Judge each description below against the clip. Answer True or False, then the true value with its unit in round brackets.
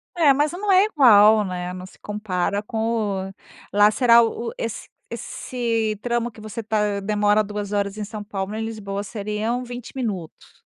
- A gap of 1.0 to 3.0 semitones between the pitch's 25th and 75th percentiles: True (2.5 semitones)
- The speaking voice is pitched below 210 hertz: False (215 Hz)